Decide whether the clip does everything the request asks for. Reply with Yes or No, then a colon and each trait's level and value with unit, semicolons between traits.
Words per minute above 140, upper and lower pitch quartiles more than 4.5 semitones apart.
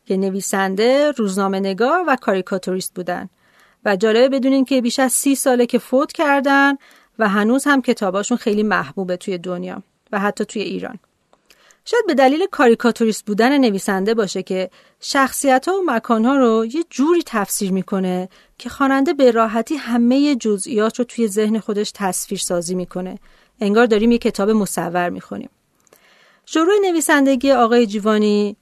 Yes: average, 150 wpm; average, 5.1 semitones